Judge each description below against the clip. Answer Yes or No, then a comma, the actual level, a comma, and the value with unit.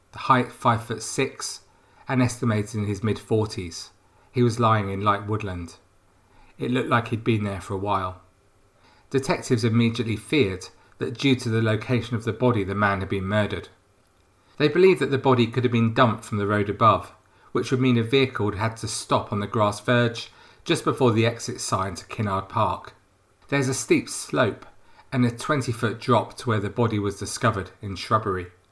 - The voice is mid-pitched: No, low, 110 Hz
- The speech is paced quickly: No, average, 195 wpm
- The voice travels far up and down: No, average, 3.3 semitones